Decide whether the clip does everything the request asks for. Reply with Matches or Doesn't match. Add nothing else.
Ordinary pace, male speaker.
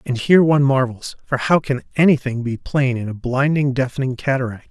Matches